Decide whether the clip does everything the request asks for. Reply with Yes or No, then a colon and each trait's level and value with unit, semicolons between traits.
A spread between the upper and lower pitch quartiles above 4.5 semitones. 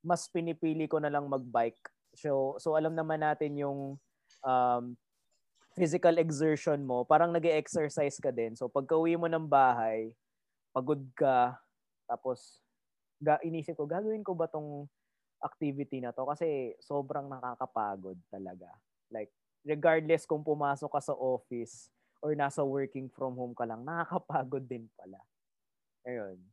No: average, 4.0 semitones